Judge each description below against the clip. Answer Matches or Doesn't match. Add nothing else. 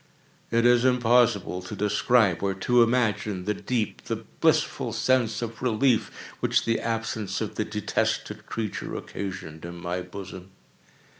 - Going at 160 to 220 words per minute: Doesn't match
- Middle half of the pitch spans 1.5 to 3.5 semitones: Doesn't match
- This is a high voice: Doesn't match